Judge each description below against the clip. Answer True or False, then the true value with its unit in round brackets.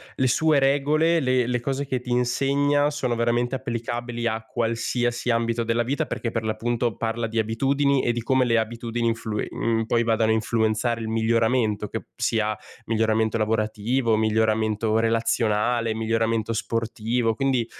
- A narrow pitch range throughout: True (1.7 semitones)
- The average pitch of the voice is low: True (115 Hz)